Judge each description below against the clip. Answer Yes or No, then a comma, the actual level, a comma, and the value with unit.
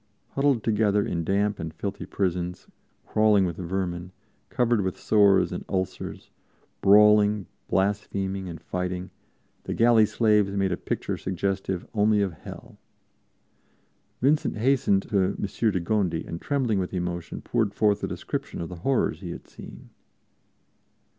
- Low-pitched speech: Yes, low, 100 Hz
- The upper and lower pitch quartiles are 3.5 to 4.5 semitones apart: No, average, 2.7 semitones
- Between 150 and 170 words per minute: No, average, 140 wpm